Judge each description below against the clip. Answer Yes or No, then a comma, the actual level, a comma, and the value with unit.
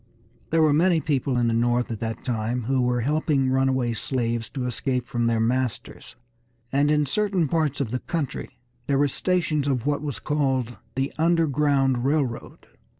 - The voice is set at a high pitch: No, low, 135 Hz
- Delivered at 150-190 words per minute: Yes, average, 170 wpm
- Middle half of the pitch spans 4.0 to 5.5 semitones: No, average, 3.5 semitones